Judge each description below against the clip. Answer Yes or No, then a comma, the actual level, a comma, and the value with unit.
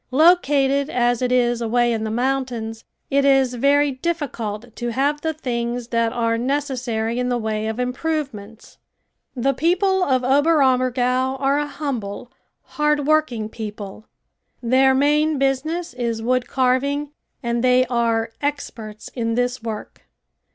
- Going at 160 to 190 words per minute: No, slow, 135 wpm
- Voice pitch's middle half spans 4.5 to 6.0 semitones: No, average, 3.2 semitones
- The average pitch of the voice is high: Yes, very high, 255 Hz